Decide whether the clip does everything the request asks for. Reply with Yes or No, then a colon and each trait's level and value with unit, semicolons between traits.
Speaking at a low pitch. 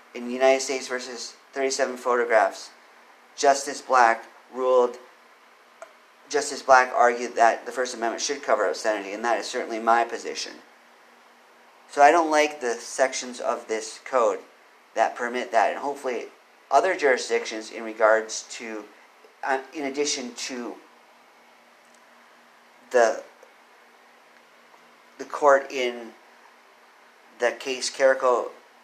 Yes: low, 125 Hz